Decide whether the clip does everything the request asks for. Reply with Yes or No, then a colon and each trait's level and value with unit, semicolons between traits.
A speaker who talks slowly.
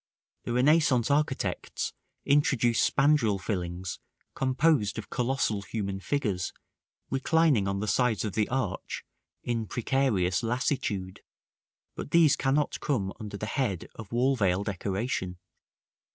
Yes: slow, 120 wpm